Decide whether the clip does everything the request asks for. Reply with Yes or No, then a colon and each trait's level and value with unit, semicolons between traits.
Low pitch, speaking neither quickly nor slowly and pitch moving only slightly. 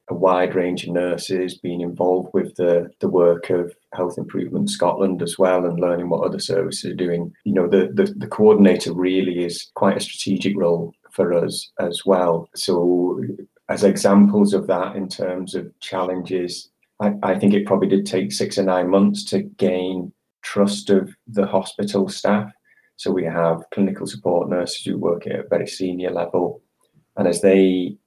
Yes: very low, 90 Hz; average, 175 wpm; narrow, 1.8 semitones